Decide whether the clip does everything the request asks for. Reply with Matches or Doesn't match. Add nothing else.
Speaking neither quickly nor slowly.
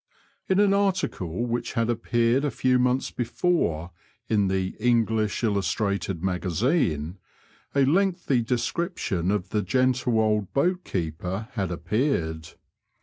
Doesn't match